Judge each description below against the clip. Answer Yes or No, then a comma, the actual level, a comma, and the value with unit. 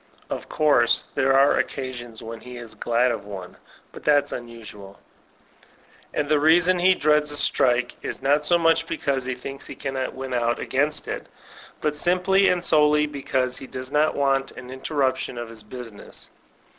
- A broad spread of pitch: No, average, 3.7 semitones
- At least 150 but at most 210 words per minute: Yes, average, 175 wpm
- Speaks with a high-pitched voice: No, low, 135 Hz